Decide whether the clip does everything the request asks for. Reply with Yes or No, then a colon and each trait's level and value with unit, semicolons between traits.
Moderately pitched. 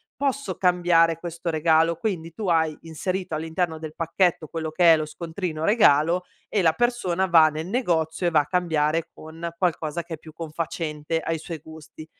Yes: medium, 165 Hz